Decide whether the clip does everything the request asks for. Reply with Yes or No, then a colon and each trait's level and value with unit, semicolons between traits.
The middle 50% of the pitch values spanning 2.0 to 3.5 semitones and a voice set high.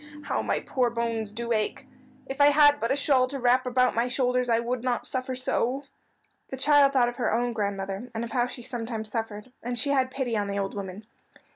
Yes: narrow, 2.4 semitones; high, 245 Hz